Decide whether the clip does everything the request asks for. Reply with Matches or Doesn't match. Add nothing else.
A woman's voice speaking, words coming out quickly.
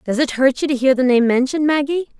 Matches